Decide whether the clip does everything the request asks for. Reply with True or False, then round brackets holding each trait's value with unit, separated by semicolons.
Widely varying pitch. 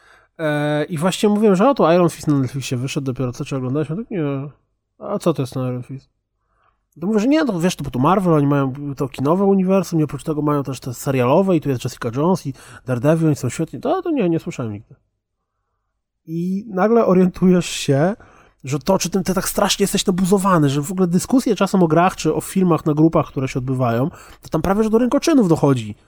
True (5.8 semitones)